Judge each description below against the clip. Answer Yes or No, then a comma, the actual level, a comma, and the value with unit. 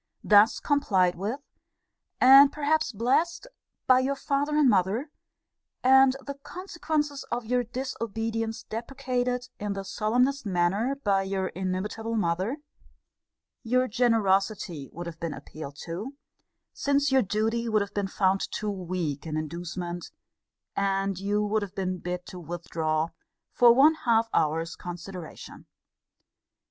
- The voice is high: Yes, high, 215 Hz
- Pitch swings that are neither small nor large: No, wide, 5.8 semitones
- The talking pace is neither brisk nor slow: No, slow, 130 wpm